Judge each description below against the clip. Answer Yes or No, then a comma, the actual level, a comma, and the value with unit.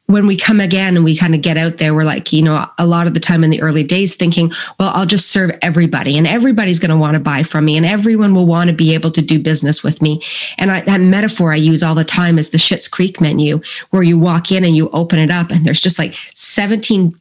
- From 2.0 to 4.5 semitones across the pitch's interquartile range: Yes, average, 2.8 semitones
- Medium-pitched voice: Yes, medium, 170 Hz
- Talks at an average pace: No, fast, 280 wpm